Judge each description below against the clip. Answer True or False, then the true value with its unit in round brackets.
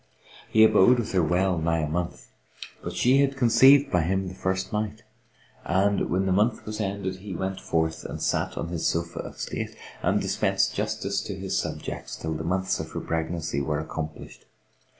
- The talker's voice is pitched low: True (95 Hz)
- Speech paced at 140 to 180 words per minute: False (190 wpm)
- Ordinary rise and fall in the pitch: True (4.1 semitones)